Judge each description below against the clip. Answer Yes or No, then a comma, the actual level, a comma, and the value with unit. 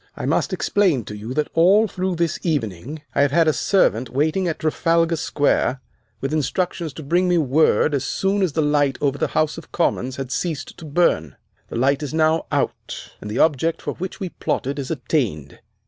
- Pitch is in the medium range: Yes, medium, 155 Hz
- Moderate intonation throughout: Yes, average, 3.8 semitones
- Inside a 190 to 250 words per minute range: Yes, average, 200 wpm